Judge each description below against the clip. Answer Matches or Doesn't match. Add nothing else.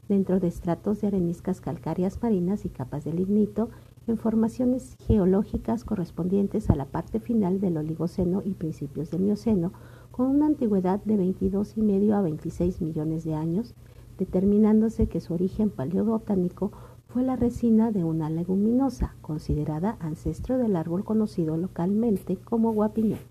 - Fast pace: Doesn't match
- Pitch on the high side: Matches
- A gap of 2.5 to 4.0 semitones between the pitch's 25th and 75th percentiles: Doesn't match